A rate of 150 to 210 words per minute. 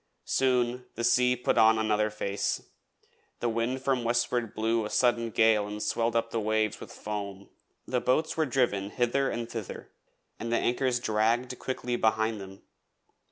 Yes: average, 160 wpm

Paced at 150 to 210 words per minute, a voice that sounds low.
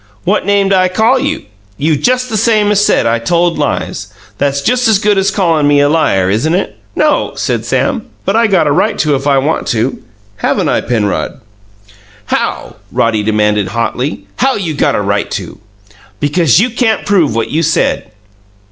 No: average, 185 wpm; medium, 165 Hz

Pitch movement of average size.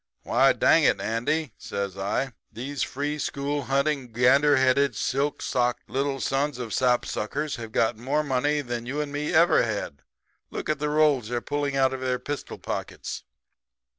Yes: average, 3.1 semitones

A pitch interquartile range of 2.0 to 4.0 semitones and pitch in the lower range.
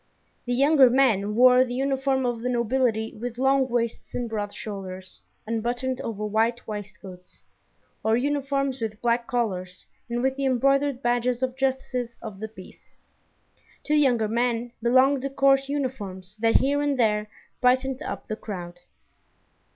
No: average, 3.4 semitones; high, 245 Hz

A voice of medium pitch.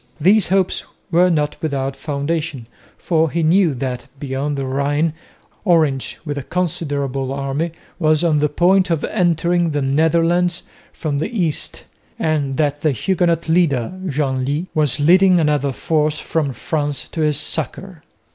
Yes: medium, 155 Hz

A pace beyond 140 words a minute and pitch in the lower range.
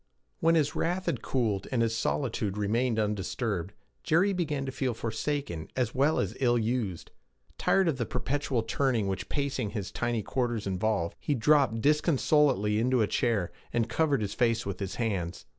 Yes: average, 170 wpm; low, 120 Hz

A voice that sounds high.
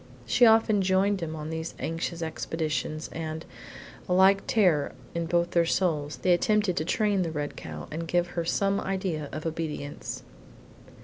No: medium, 170 Hz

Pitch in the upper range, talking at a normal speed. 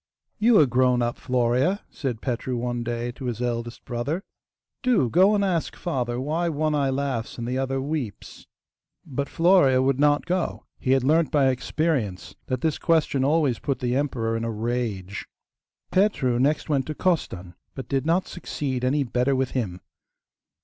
No: low, 130 Hz; average, 170 wpm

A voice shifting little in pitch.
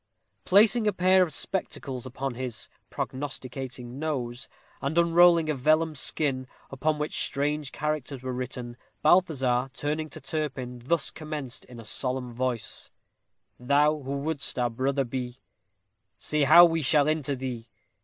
No: average, 3.5 semitones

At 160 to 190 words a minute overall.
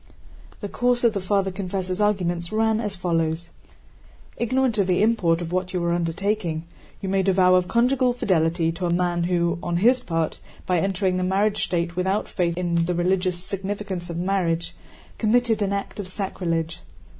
Yes: average, 180 wpm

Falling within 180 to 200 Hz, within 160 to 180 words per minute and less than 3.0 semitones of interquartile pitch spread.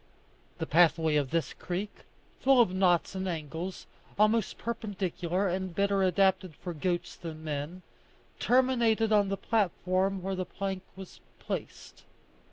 No: medium, 185 Hz; slow, 135 wpm; narrow, 2.5 semitones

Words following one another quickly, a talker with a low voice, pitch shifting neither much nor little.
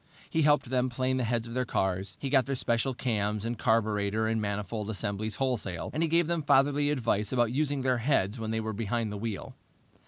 Yes: fast, 215 wpm; low, 115 Hz; average, 3.8 semitones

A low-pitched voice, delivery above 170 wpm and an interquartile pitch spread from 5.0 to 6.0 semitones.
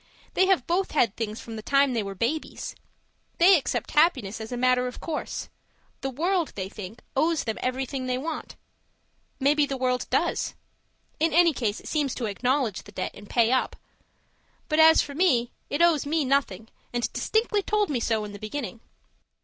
No: very high, 260 Hz; average, 185 wpm; wide, 5.4 semitones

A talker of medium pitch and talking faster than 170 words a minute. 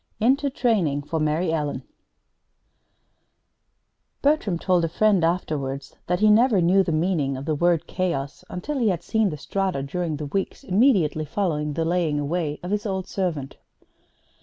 No: medium, 175 Hz; average, 160 wpm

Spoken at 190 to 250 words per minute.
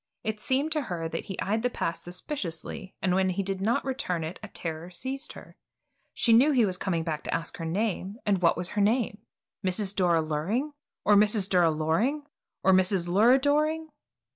Yes: average, 195 wpm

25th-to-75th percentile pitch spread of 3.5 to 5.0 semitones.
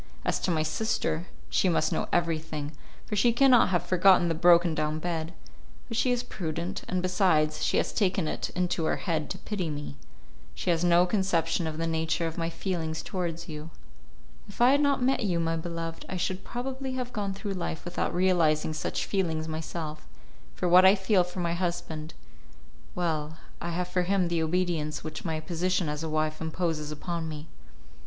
No: average, 2.7 semitones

